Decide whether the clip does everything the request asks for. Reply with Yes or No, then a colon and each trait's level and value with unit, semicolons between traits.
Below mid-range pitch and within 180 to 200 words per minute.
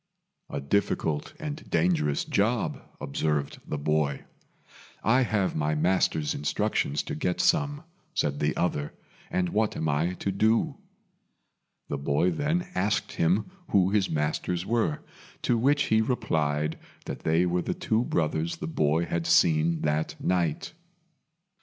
No: very low, 85 Hz; average, 140 wpm